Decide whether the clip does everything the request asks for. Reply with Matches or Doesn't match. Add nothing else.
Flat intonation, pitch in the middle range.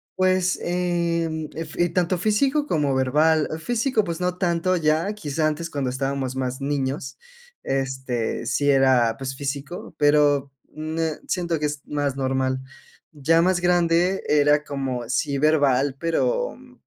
Doesn't match